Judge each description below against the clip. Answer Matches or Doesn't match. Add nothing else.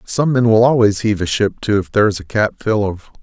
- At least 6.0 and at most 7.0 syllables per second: Matches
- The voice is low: Matches